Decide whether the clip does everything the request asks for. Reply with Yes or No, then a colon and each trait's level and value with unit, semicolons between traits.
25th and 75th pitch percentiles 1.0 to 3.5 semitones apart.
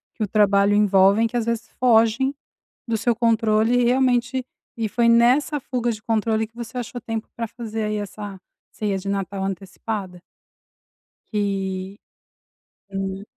Yes: average, 2.9 semitones